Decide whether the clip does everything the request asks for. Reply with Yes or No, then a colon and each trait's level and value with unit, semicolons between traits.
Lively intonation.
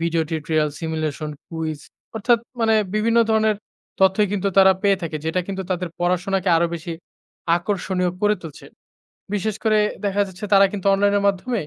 No: average, 3.5 semitones